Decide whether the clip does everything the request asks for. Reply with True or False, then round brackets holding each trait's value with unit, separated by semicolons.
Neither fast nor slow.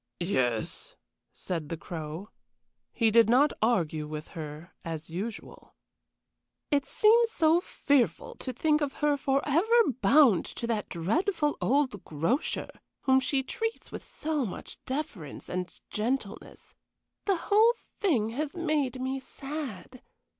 False (125 wpm)